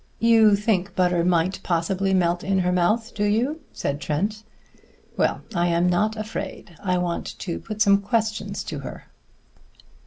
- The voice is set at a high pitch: Yes, high, 195 Hz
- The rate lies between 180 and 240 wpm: No, average, 155 wpm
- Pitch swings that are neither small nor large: Yes, average, 3.4 semitones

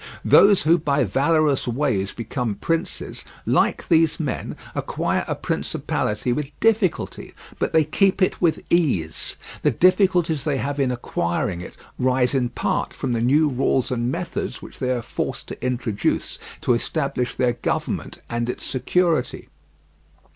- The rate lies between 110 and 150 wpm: Yes, average, 145 wpm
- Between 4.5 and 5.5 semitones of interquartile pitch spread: Yes, average, 4.8 semitones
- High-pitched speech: No, low, 135 Hz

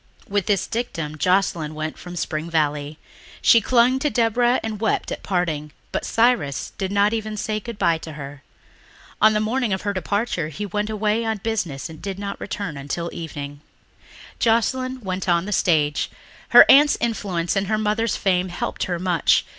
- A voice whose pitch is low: No, high, 195 Hz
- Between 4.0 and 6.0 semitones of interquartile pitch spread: Yes, average, 5.2 semitones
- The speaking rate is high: No, average, 175 wpm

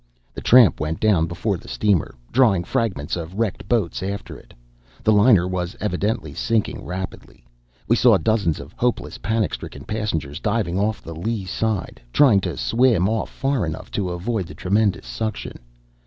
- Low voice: Yes, low, 100 Hz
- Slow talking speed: No, average, 165 wpm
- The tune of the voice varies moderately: Yes, average, 4.1 semitones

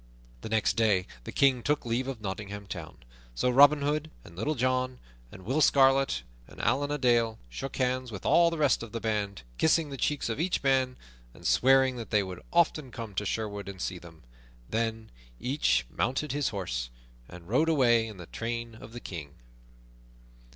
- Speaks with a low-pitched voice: Yes, low, 120 Hz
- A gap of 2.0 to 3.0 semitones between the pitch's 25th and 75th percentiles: No, average, 4.9 semitones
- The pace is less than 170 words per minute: No, average, 185 wpm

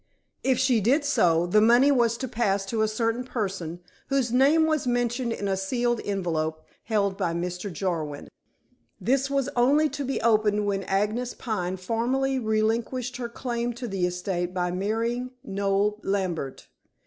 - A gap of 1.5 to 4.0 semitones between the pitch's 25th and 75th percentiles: No, average, 4.5 semitones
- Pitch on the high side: Yes, high, 220 Hz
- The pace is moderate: Yes, average, 160 wpm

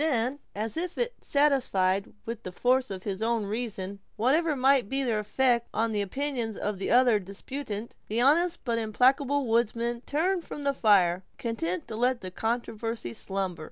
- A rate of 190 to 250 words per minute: No, average, 165 wpm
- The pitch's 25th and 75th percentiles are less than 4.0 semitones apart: No, average, 4.5 semitones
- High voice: Yes, high, 230 Hz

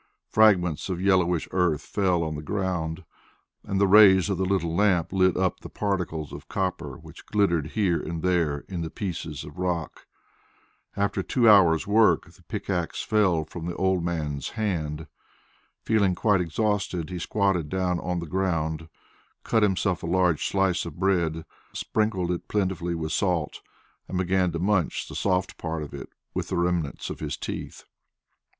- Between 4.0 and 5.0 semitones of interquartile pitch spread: No, average, 2.8 semitones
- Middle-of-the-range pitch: No, very low, 90 Hz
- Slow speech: No, average, 165 wpm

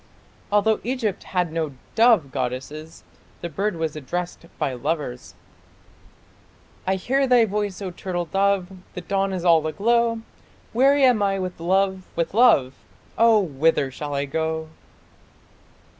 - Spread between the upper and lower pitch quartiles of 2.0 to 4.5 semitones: No, average, 4.9 semitones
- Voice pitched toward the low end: No, medium, 185 Hz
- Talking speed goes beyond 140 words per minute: No, slow, 135 wpm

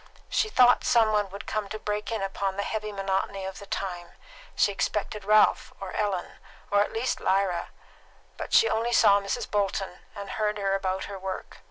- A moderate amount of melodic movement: No, narrow, 1.6 semitones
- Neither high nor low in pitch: No, high, 200 Hz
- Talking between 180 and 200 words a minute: Yes, average, 190 wpm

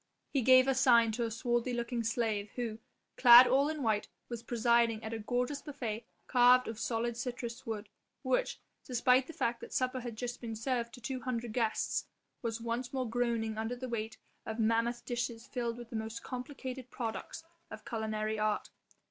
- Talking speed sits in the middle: Yes, average, 180 wpm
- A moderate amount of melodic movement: No, narrow, 1.9 semitones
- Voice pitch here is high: Yes, high, 235 Hz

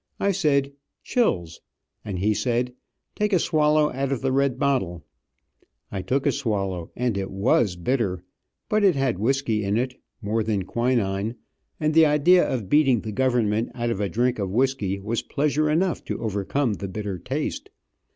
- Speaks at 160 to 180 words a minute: Yes, average, 170 wpm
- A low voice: Yes, low, 120 Hz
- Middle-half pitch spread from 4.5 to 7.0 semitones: Yes, wide, 5.5 semitones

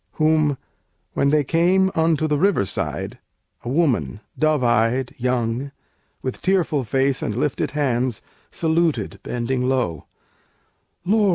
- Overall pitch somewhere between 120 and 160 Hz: Yes, medium, 140 Hz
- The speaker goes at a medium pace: No, slow, 120 wpm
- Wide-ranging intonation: No, average, 4.6 semitones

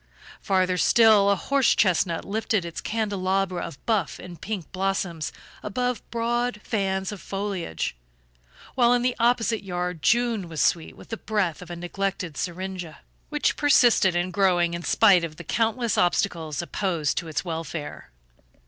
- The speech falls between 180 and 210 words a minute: No, average, 150 wpm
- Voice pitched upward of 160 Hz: Yes, high, 190 Hz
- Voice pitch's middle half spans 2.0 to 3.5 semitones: No, average, 4.3 semitones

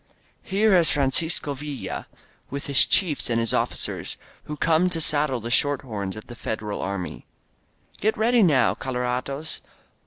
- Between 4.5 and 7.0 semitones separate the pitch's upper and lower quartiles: Yes, average, 5.1 semitones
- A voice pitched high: No, medium, 140 Hz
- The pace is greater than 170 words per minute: No, average, 150 wpm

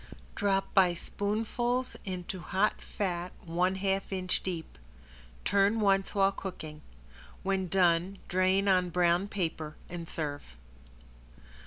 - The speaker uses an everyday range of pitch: No, narrow, 2.2 semitones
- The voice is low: No, medium, 185 Hz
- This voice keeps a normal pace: No, slow, 115 wpm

